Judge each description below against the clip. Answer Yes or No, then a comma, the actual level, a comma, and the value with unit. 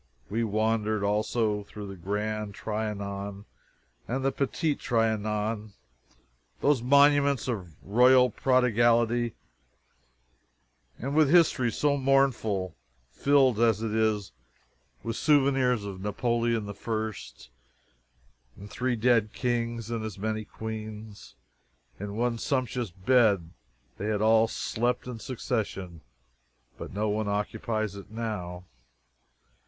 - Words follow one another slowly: Yes, slow, 110 wpm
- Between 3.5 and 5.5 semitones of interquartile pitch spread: No, average, 2.9 semitones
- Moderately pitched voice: No, low, 110 Hz